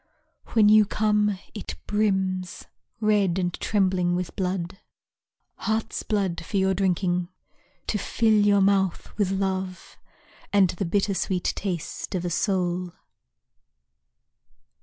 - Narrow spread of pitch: Yes, narrow, 2.3 semitones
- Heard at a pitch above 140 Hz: Yes, high, 190 Hz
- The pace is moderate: No, slow, 115 wpm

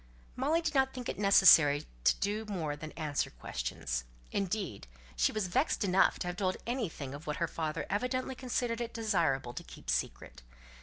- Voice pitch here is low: No, high, 195 Hz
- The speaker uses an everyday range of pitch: No, wide, 7.8 semitones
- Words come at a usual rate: Yes, average, 175 wpm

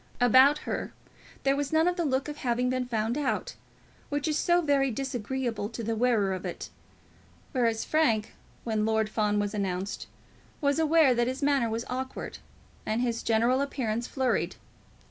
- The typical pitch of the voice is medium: No, very high, 250 Hz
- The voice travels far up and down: No, average, 4.0 semitones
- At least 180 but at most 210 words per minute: No, average, 165 wpm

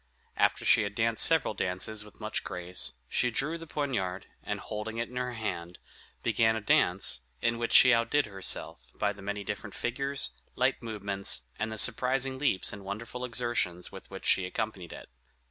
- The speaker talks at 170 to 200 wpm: Yes, average, 180 wpm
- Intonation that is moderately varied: Yes, average, 4.1 semitones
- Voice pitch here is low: Yes, low, 110 Hz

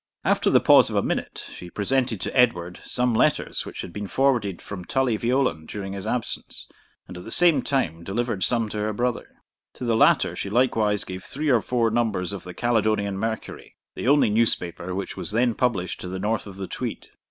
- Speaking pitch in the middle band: No, low, 110 Hz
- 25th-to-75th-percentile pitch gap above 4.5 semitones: No, average, 4.1 semitones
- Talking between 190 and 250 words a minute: Yes, fast, 205 wpm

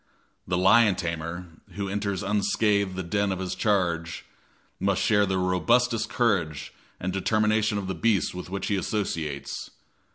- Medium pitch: No, very low, 95 Hz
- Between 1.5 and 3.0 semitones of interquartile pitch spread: Yes, narrow, 2.5 semitones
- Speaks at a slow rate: No, average, 150 wpm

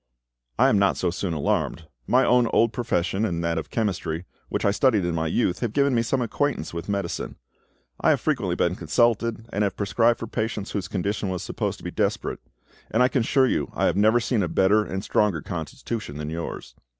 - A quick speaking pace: Yes, fast, 210 wpm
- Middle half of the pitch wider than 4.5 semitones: Yes, average, 4.9 semitones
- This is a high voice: No, low, 105 Hz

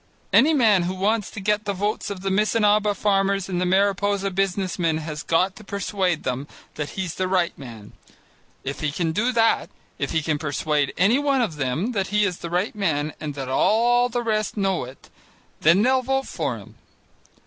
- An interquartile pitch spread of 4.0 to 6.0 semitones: Yes, average, 4.8 semitones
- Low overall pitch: No, high, 190 Hz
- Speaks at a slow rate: No, average, 200 wpm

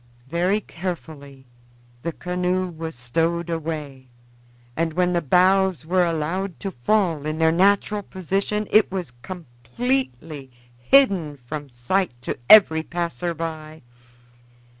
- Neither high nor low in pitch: Yes, medium, 170 Hz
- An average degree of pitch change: Yes, average, 3.6 semitones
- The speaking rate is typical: No, slow, 120 wpm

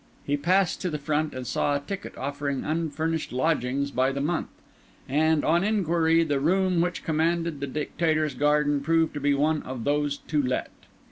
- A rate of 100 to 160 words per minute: No, average, 180 wpm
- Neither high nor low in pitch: Yes, medium, 150 Hz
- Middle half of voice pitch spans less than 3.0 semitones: Yes, narrow, 2.6 semitones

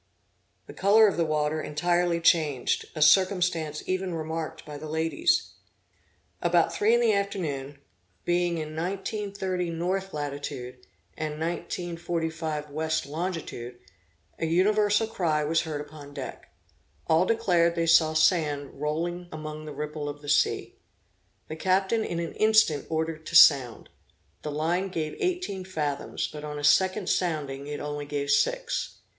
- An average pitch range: Yes, average, 3.6 semitones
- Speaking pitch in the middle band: Yes, medium, 160 Hz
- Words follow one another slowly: No, average, 145 wpm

